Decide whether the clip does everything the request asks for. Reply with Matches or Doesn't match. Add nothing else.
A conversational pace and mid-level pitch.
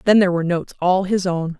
Doesn't match